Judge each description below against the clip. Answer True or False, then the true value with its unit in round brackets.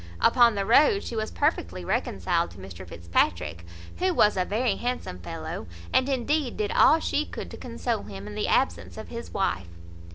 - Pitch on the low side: False (195 Hz)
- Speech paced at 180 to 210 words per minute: True (185 wpm)